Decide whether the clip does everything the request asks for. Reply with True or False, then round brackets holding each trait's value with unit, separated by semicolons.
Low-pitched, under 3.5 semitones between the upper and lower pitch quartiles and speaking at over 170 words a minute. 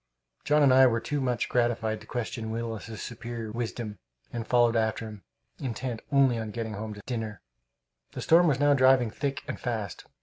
True (120 Hz; 2.8 semitones; 180 wpm)